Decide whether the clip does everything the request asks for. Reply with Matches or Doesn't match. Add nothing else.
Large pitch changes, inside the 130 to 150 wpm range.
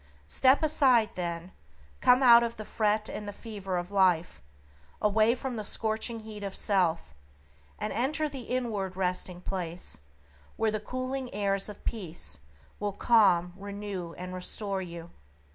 Doesn't match